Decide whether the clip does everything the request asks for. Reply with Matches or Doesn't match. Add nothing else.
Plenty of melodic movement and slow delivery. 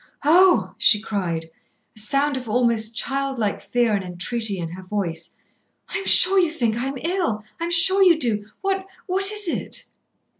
Doesn't match